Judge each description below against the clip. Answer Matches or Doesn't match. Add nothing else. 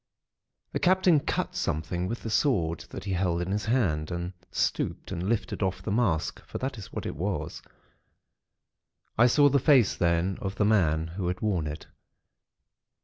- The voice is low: Matches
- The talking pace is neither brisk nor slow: Matches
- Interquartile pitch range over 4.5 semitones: Matches